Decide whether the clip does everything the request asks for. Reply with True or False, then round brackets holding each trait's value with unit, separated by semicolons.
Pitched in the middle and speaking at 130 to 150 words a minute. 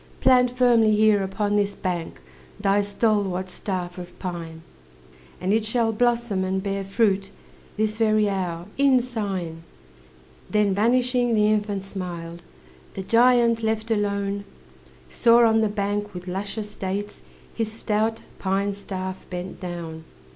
False (205 Hz; 135 wpm)